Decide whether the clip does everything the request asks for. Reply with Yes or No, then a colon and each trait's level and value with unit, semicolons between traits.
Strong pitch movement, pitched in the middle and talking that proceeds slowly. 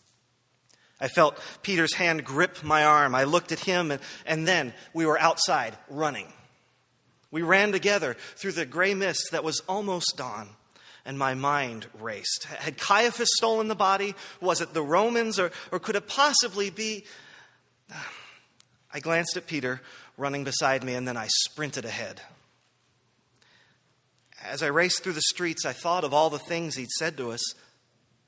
No: wide, 6.0 semitones; medium, 160 Hz; average, 160 wpm